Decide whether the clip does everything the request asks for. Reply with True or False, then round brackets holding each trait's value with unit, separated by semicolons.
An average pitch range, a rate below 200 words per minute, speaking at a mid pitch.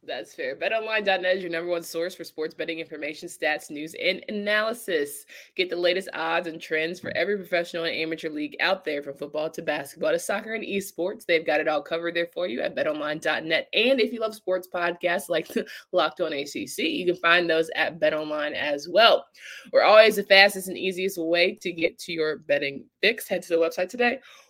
False (3.5 semitones; 205 wpm; 175 Hz)